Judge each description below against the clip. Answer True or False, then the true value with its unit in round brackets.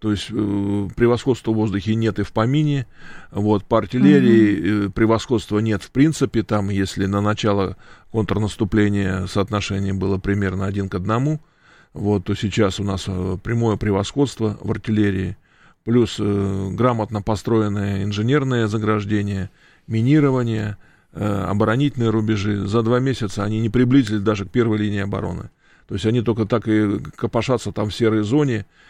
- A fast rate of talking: False (145 wpm)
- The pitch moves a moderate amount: False (2.3 semitones)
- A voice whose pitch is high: False (105 Hz)